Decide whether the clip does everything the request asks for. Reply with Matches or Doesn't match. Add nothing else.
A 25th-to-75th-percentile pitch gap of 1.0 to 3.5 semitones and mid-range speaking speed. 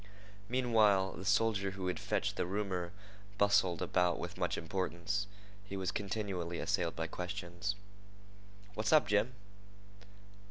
Doesn't match